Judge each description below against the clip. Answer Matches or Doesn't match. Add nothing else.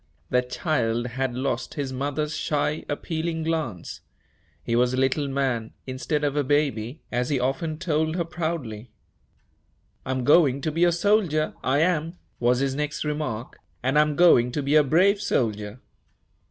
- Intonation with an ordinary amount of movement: Matches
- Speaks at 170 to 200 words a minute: Doesn't match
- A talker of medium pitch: Matches